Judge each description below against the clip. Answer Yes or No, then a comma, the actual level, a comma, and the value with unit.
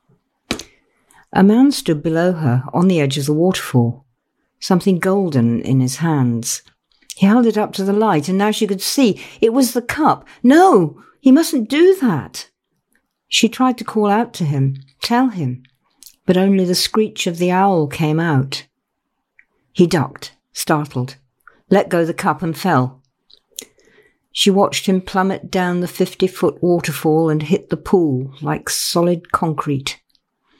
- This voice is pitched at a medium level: Yes, medium, 180 Hz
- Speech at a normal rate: Yes, average, 155 wpm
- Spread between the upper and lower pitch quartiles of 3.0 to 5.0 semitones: No, wide, 5.5 semitones